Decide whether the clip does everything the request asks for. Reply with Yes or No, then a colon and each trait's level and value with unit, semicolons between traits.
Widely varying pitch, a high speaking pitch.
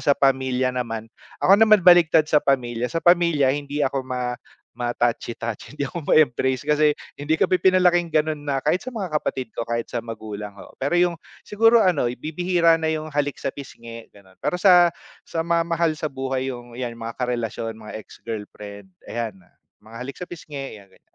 No: wide, 5.8 semitones; medium, 140 Hz